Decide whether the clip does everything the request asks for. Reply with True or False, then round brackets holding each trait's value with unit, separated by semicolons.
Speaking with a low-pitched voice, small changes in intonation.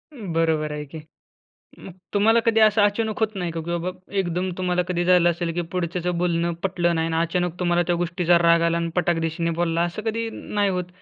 False (175 Hz; 1.8 semitones)